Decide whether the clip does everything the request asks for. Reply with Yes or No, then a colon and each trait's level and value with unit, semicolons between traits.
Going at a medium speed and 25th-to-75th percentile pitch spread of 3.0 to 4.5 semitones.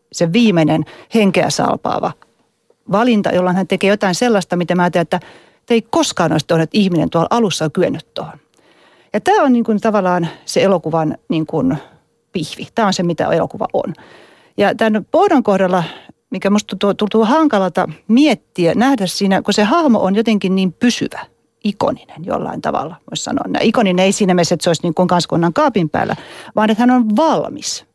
No: fast, 175 wpm; average, 4.0 semitones